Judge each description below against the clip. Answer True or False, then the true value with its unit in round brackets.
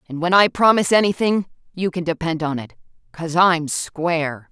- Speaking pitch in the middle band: True (170 Hz)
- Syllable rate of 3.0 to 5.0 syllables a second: False (5.2 syllables/s)